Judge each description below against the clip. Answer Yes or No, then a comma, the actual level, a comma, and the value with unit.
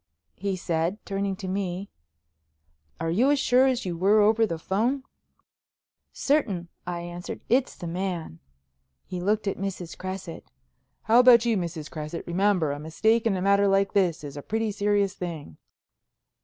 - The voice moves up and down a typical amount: Yes, average, 3.7 semitones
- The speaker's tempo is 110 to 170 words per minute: Yes, average, 160 wpm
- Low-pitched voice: No, high, 195 Hz